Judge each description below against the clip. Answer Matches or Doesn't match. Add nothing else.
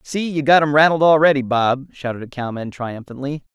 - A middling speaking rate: Matches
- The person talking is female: Doesn't match